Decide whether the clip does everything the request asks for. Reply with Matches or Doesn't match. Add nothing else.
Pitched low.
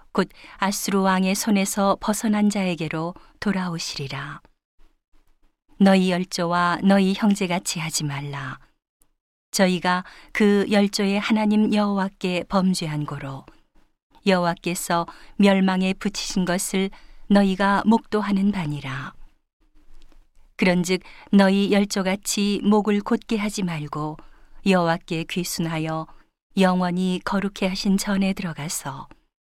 Doesn't match